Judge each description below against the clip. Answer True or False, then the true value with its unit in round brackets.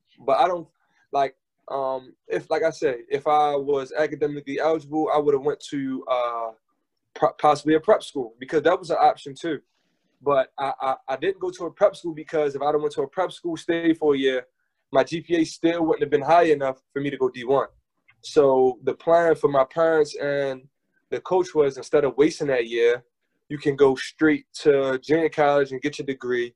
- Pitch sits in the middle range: True (155 Hz)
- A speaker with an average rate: False (210 wpm)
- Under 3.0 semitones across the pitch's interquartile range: False (4.5 semitones)